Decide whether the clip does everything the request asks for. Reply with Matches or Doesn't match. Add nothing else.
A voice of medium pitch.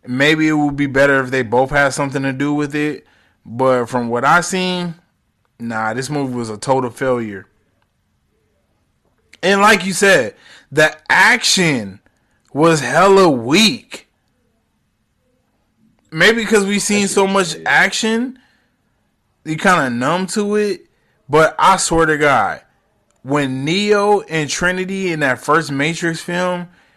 Matches